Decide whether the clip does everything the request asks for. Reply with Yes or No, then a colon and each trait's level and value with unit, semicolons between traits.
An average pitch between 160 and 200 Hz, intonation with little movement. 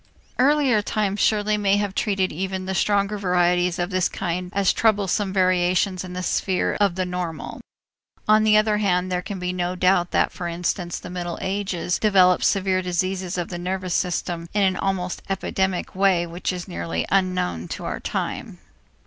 Yes: medium, 185 Hz; narrow, 1.9 semitones